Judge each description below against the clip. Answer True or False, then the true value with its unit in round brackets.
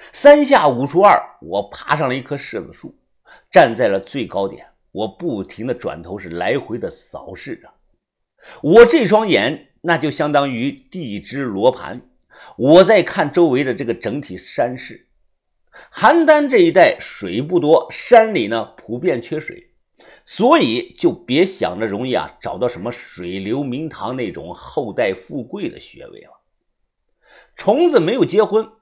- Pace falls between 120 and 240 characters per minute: True (220 characters per minute)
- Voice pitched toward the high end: True (215 Hz)